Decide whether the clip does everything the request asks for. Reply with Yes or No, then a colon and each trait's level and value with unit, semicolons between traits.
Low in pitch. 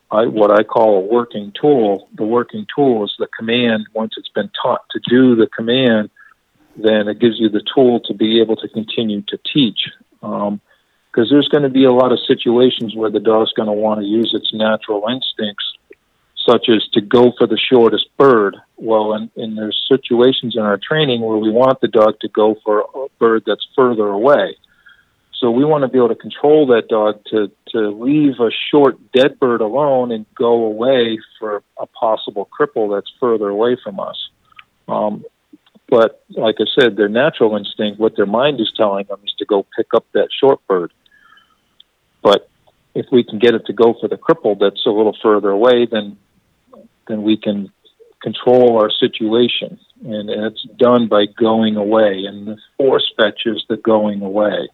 Yes: low, 110 Hz